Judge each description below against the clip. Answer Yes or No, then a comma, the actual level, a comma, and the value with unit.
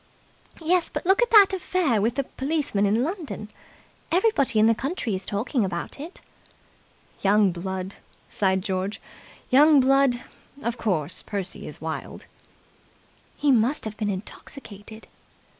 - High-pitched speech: Yes, high, 230 Hz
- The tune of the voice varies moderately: No, wide, 6.6 semitones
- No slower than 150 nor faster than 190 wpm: No, slow, 135 wpm